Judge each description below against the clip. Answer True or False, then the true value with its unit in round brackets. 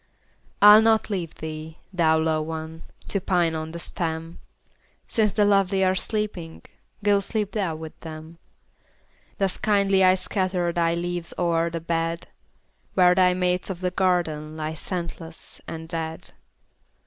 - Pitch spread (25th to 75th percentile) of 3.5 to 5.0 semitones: False (2.7 semitones)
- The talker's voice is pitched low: False (175 Hz)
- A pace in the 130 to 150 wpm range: True (145 wpm)